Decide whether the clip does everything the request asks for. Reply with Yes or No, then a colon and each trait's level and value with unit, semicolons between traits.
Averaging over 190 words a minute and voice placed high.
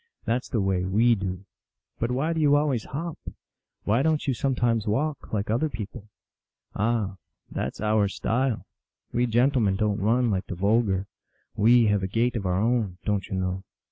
No: fast, 205 wpm; low, 110 Hz